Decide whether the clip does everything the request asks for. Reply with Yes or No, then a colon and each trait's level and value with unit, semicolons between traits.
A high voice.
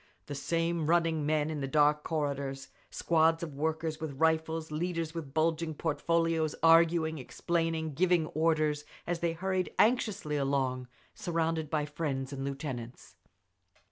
No: medium, 160 Hz